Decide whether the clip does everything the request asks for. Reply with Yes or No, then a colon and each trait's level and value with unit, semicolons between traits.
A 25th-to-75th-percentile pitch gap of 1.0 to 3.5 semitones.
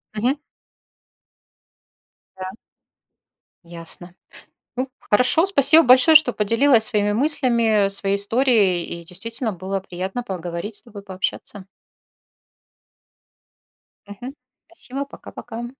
No: average, 4.8 semitones